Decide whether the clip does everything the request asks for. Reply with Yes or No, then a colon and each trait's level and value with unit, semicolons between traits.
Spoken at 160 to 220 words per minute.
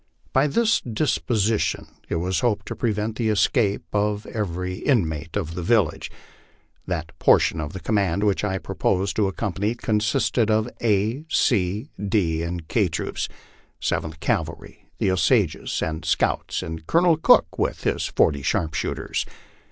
No: average, 145 wpm